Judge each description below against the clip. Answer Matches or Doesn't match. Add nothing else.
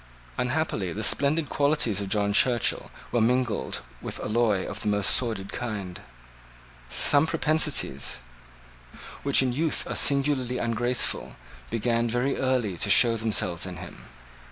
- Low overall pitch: Matches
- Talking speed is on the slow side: Matches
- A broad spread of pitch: Doesn't match